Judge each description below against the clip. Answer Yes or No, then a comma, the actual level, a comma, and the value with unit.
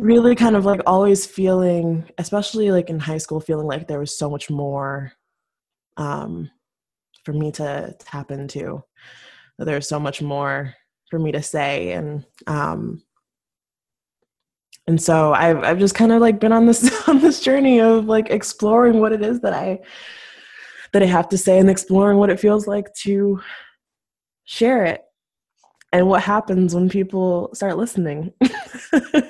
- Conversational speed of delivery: Yes, average, 160 wpm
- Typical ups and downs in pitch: No, wide, 5.9 semitones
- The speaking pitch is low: No, medium, 185 Hz